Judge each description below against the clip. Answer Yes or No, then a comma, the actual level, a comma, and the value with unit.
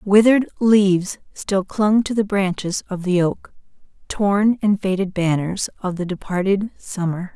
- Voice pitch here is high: Yes, high, 195 Hz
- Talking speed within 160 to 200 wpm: No, average, 145 wpm